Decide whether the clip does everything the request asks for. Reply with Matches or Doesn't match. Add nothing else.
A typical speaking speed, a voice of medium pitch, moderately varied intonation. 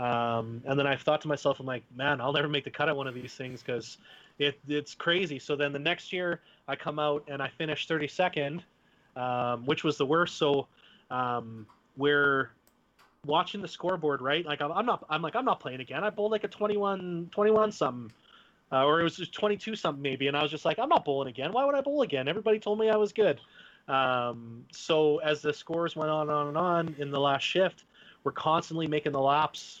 Doesn't match